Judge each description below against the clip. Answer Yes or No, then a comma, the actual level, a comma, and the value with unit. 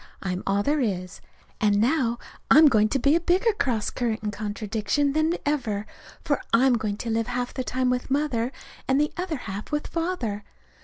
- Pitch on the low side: No, high, 245 Hz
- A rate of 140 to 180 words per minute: No, average, 190 wpm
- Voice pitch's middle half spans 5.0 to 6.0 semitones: Yes, wide, 5.5 semitones